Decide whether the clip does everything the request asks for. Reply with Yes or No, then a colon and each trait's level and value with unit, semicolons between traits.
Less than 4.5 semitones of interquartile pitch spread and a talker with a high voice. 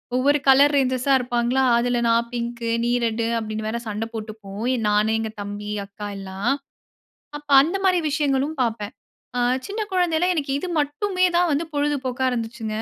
No: average, 4.8 semitones; high, 245 Hz